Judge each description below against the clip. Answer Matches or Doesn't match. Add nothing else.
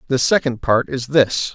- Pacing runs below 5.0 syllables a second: Matches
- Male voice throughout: Matches